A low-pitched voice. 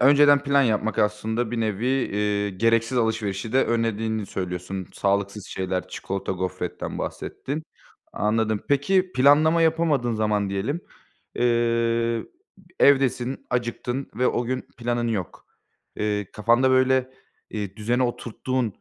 Yes: low, 115 Hz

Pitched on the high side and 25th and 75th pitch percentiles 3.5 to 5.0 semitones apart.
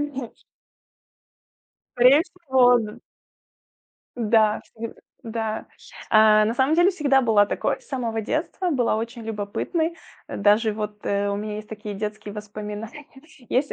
Yes: high, 225 Hz; average, 3.9 semitones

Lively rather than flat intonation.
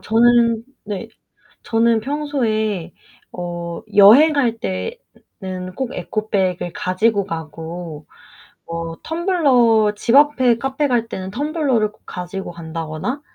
Yes: wide, 5.8 semitones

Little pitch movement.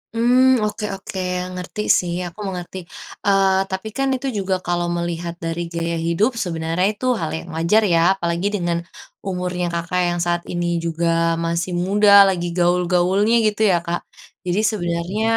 Yes: narrow, 2.3 semitones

